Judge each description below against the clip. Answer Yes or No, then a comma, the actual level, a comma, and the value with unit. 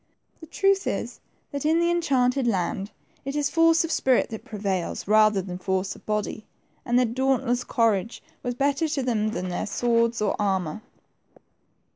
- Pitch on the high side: Yes, high, 235 Hz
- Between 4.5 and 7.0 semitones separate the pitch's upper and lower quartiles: Yes, average, 5.2 semitones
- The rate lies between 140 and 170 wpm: Yes, average, 165 wpm